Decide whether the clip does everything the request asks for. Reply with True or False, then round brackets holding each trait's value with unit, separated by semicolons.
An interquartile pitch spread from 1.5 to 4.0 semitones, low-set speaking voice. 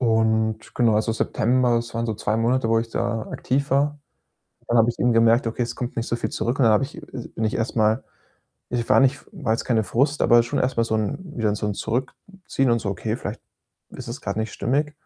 True (2.4 semitones; 115 Hz)